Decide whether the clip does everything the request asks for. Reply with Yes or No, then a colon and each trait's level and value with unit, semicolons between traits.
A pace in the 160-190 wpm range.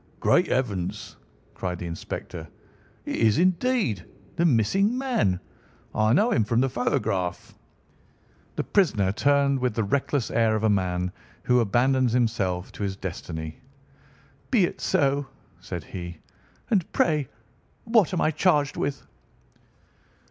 No: slow, 135 wpm